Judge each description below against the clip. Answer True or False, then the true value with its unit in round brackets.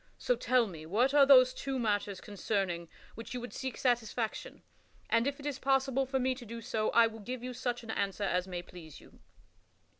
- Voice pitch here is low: False (235 Hz)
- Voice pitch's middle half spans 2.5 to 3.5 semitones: False (4.2 semitones)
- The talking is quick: True (210 wpm)